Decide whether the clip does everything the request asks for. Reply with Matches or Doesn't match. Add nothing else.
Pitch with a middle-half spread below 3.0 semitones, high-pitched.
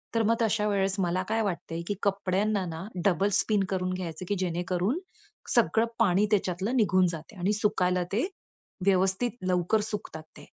Matches